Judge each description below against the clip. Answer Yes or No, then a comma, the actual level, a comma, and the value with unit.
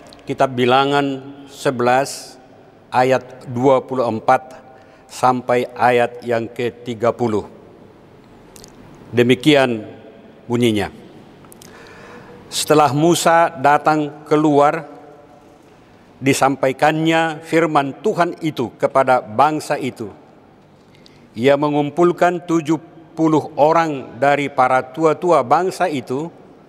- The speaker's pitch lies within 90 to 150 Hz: Yes, medium, 140 Hz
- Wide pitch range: No, average, 3.2 semitones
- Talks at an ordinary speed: No, slow, 70 wpm